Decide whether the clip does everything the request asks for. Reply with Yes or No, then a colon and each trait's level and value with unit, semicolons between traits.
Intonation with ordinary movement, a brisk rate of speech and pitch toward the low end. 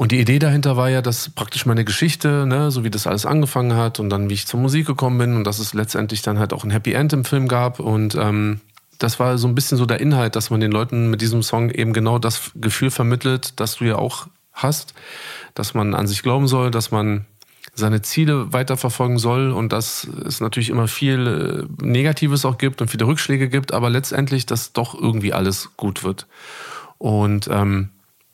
Yes: average, 3.5 semitones; fast, 210 wpm; low, 120 Hz